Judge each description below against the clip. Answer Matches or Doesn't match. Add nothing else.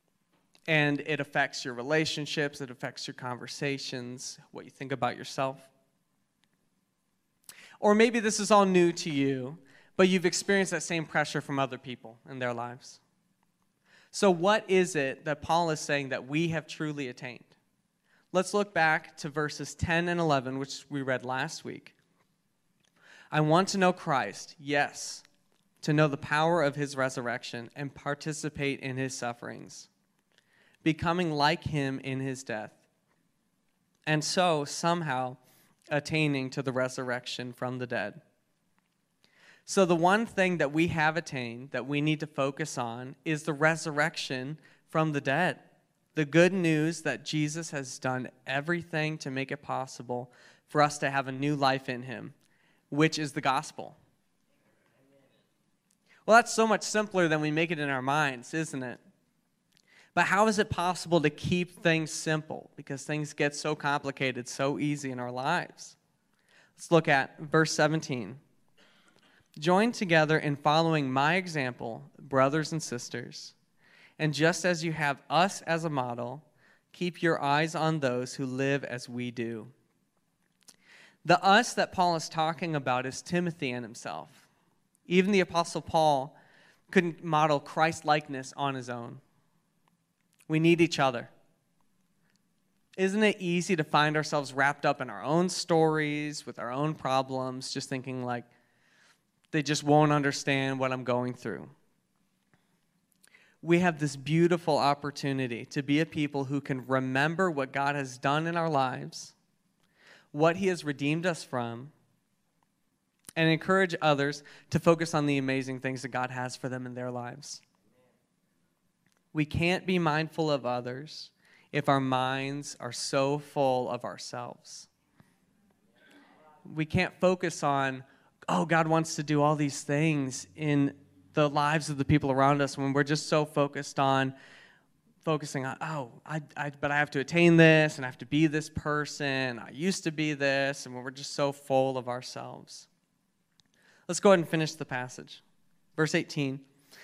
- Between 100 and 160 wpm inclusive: Matches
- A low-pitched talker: Doesn't match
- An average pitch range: Matches